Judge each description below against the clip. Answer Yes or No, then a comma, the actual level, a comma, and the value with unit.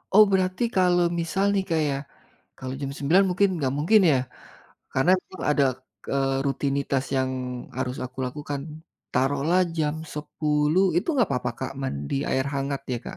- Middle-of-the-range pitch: Yes, medium, 145 Hz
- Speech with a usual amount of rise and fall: Yes, average, 4.7 semitones